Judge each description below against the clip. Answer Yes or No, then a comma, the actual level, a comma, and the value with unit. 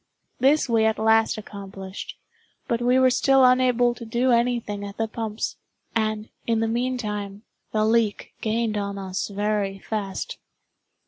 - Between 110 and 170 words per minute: Yes, average, 145 wpm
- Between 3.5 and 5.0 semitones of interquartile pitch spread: No, average, 2.7 semitones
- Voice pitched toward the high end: Yes, high, 220 Hz